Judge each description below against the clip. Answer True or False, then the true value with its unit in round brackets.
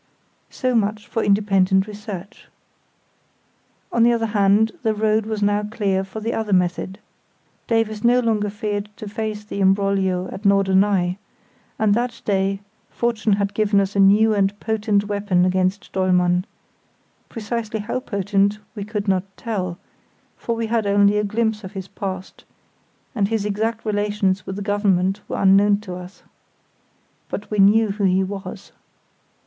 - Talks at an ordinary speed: True (155 wpm)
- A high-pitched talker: True (205 Hz)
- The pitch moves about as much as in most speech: False (1.9 semitones)